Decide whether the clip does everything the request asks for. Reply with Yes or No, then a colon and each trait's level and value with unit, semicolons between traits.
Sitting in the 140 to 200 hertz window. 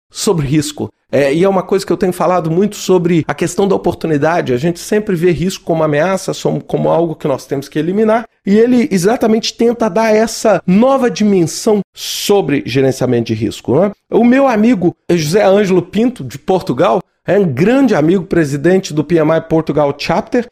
Yes: medium, 185 Hz